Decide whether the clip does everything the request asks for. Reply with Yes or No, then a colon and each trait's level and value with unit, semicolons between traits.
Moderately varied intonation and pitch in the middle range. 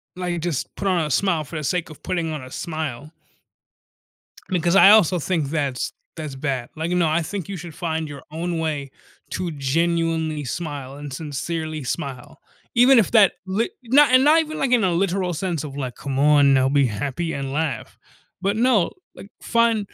Yes: average, 4.3 semitones; medium, 160 Hz